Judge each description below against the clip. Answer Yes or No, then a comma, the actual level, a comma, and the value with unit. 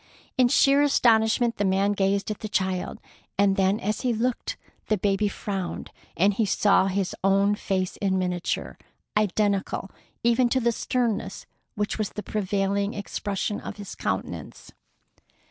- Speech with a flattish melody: Yes, narrow, 2.1 semitones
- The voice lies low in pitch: No, high, 205 Hz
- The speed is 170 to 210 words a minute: No, average, 145 wpm